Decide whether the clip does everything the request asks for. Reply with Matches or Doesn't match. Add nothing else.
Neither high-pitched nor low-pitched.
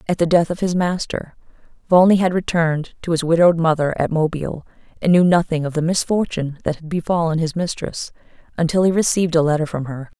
Matches